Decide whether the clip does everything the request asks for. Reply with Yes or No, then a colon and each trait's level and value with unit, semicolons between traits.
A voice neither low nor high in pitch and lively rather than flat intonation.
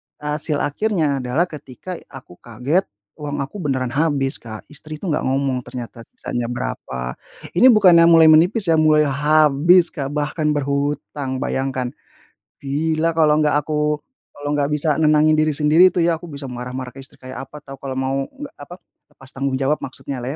No: medium, 145 Hz; average, 2.9 semitones